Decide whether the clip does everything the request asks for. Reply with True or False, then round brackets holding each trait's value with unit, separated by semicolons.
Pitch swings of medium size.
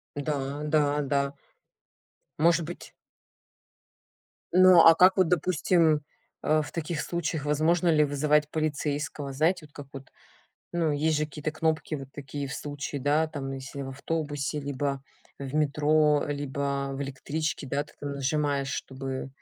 False (2.0 semitones)